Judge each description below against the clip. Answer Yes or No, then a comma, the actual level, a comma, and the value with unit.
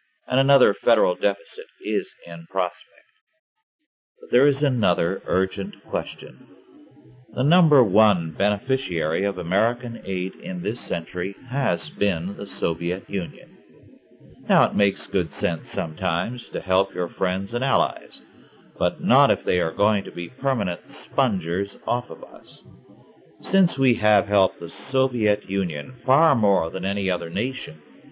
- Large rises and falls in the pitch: Yes, wide, 6.1 semitones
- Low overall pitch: Yes, low, 105 Hz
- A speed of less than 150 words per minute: Yes, average, 140 wpm